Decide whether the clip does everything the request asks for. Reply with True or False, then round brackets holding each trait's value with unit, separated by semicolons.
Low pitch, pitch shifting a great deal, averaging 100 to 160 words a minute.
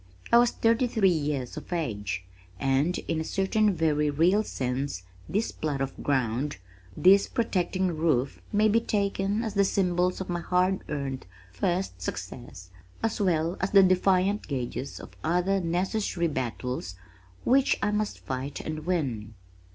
False (170 Hz; 6.3 semitones; 150 wpm)